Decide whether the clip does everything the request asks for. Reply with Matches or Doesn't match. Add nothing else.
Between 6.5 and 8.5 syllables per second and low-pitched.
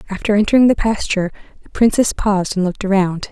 Doesn't match